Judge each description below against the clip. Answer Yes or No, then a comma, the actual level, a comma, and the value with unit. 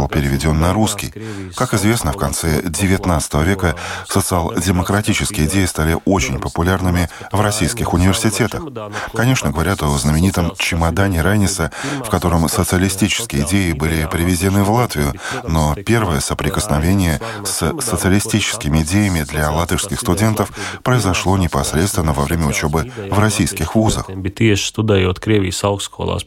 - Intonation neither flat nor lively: Yes, average, 4.5 semitones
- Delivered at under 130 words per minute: Yes, slow, 110 wpm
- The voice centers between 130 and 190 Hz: No, very low, 90 Hz